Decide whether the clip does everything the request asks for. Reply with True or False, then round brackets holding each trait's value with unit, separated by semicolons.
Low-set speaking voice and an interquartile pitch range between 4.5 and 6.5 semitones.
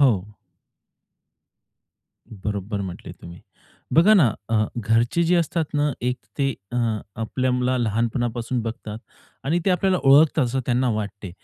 True (120 Hz; 4.8 semitones)